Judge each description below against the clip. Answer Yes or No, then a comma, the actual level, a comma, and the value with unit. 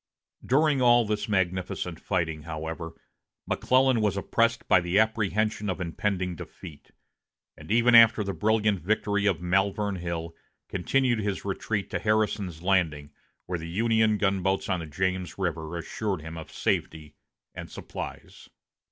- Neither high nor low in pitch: No, very low, 95 Hz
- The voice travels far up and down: No, average, 3.9 semitones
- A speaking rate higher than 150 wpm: No, average, 140 wpm